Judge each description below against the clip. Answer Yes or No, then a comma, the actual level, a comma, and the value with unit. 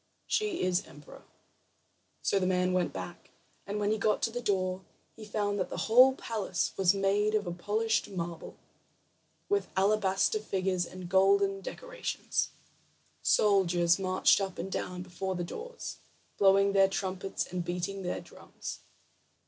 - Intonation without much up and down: Yes, narrow, 2.3 semitones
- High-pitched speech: Yes, high, 195 Hz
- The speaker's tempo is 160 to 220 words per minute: No, average, 145 wpm